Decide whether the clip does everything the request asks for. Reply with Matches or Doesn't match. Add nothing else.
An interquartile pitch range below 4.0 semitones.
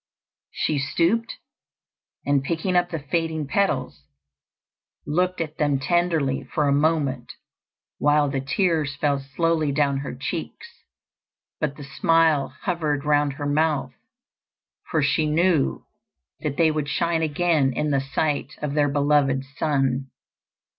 Matches